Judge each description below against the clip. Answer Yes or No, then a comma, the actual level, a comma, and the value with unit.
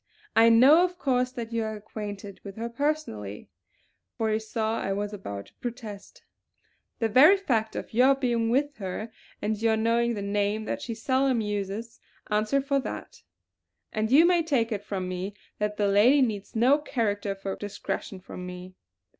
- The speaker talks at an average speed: Yes, average, 175 wpm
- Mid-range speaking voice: No, high, 220 Hz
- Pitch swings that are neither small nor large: Yes, average, 3.6 semitones